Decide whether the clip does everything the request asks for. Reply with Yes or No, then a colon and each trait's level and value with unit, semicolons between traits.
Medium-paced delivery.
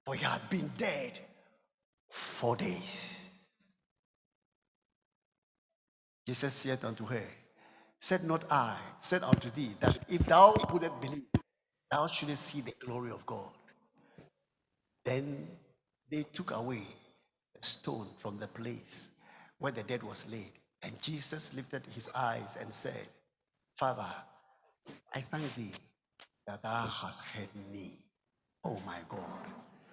No: slow, 125 wpm